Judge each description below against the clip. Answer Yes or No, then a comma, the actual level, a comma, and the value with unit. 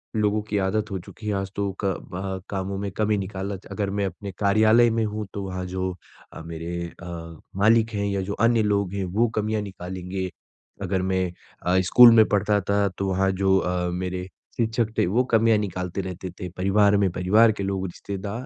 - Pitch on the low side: Yes, low, 100 Hz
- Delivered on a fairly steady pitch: Yes, narrow, 2.3 semitones